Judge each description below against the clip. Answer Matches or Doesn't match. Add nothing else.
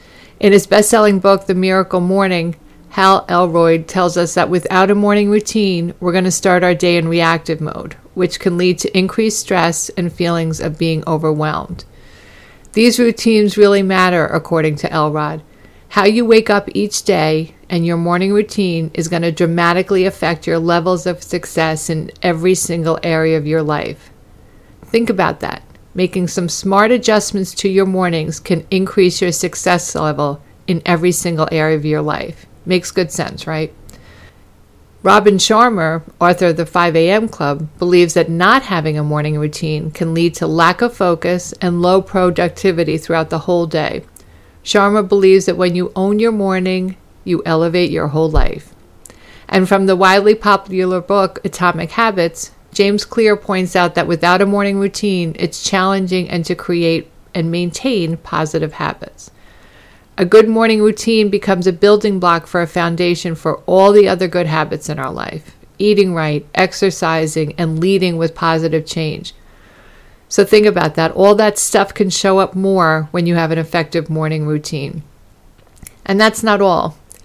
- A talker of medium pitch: Matches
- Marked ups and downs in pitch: Doesn't match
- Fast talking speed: Doesn't match